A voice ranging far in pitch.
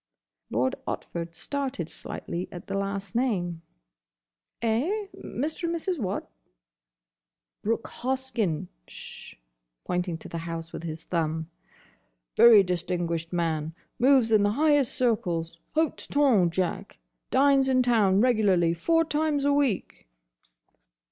Yes: wide, 7.6 semitones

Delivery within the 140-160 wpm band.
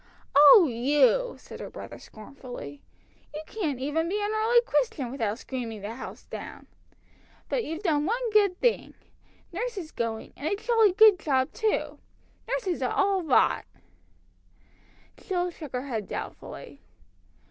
Yes: average, 145 wpm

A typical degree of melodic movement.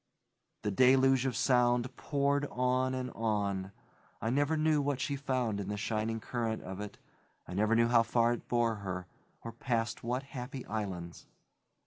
Yes: average, 3.3 semitones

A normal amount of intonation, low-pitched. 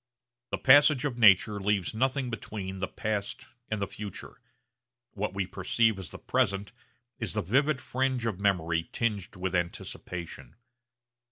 Yes: average, 4.3 semitones; low, 105 Hz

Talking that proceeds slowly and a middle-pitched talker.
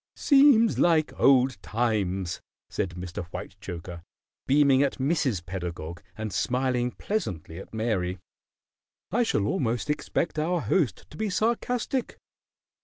No: slow, 115 wpm; low, 125 Hz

